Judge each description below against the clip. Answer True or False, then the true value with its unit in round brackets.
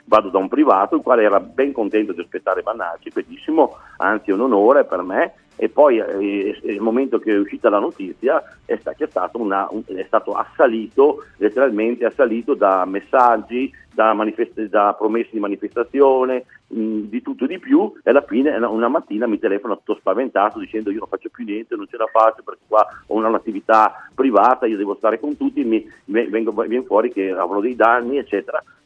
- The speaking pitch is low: True (120 Hz)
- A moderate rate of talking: False (185 wpm)